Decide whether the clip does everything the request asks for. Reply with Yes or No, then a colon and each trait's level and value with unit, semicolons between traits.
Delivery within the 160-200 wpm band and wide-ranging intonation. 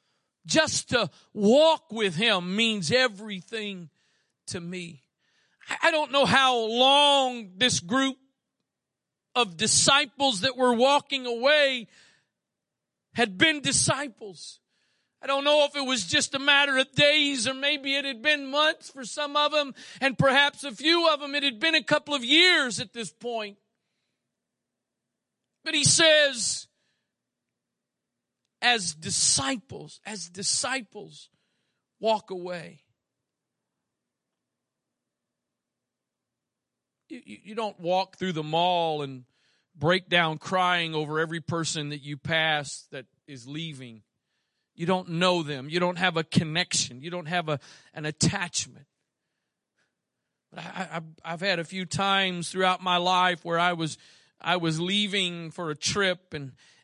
No: slow, 135 wpm; wide, 8.1 semitones